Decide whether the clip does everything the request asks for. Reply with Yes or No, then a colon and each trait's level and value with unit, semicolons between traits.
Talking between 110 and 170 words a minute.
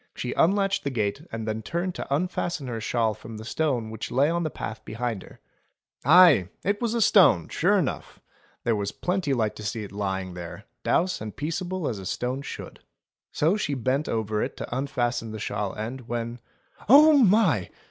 No: average, 195 wpm